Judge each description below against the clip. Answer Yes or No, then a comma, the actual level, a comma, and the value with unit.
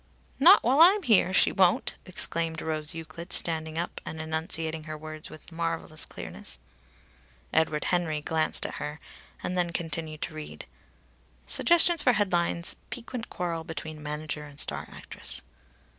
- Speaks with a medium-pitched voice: Yes, medium, 165 Hz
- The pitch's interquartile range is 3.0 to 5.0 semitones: No, narrow, 2.4 semitones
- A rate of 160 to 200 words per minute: No, average, 145 wpm